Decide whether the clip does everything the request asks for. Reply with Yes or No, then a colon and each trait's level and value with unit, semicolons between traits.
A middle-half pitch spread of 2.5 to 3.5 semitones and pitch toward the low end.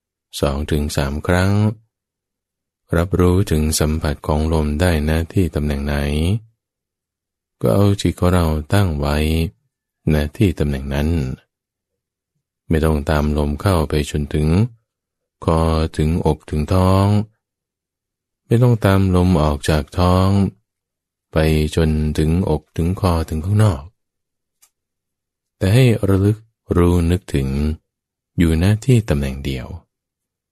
No: average, 4.0 semitones; very low, 80 Hz